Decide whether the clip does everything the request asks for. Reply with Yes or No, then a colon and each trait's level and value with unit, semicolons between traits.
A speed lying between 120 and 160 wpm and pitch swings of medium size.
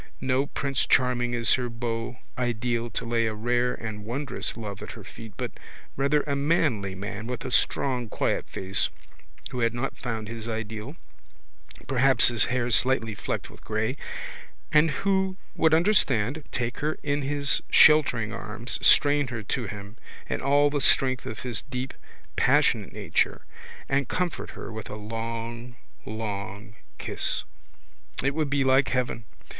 Yes: average, 155 wpm; average, 3.5 semitones